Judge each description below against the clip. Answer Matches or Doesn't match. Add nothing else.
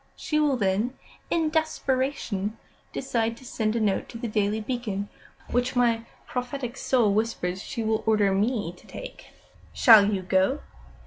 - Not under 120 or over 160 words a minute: Matches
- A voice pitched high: Matches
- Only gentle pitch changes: Doesn't match